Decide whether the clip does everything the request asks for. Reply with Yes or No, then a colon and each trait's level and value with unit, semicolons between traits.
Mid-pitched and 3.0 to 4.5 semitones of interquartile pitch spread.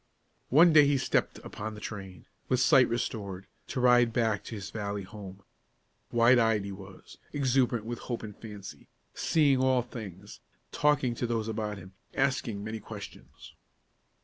No: low, 115 Hz; average, 3.8 semitones